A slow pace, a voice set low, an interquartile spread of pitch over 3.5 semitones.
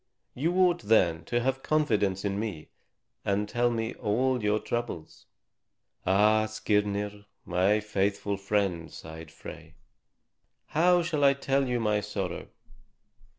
Yes: slow, 125 wpm; low, 105 Hz; average, 3.9 semitones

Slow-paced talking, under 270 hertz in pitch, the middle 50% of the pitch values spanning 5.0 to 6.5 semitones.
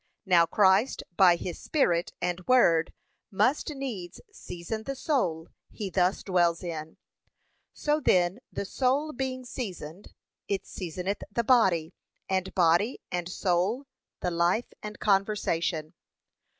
Yes: slow, 125 wpm; high, 190 Hz; wide, 5.4 semitones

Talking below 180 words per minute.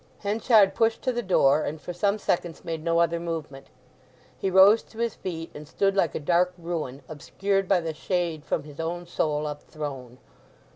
No: average, 190 wpm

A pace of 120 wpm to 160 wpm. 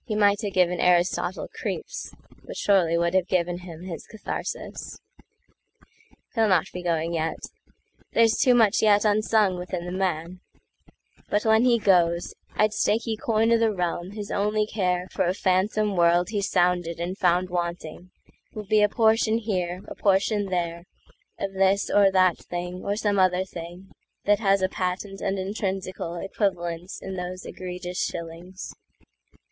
Yes: average, 140 wpm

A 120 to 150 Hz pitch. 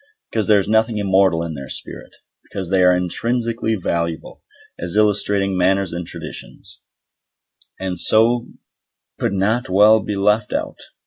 No: low, 100 Hz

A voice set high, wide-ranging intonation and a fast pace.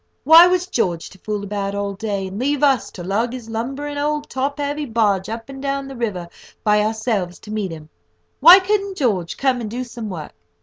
Yes: high, 230 Hz; wide, 5.7 semitones; fast, 210 wpm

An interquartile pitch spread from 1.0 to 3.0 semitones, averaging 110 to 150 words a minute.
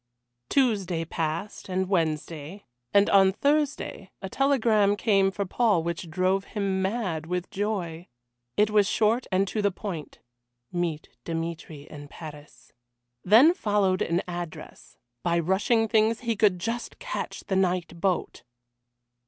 No: average, 3.9 semitones; slow, 135 wpm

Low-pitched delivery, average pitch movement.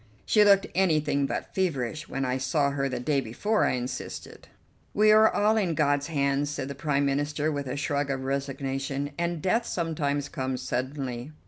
No: medium, 145 Hz; average, 3.1 semitones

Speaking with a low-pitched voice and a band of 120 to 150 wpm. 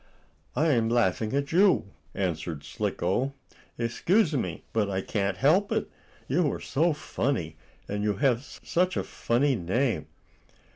Yes: low, 115 Hz; average, 140 wpm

